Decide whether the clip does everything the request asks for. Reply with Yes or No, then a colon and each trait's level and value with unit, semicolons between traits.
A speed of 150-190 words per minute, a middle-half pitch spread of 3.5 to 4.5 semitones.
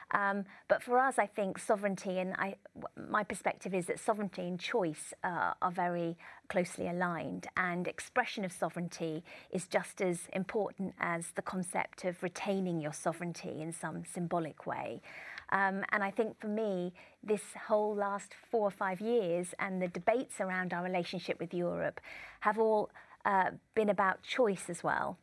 No: average, 165 wpm; average, 2.9 semitones